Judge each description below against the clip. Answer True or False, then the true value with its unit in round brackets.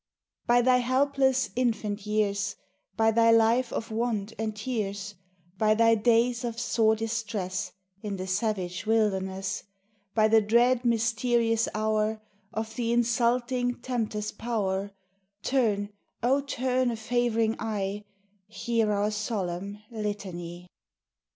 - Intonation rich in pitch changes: False (2.4 semitones)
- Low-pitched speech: False (220 Hz)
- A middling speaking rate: False (120 wpm)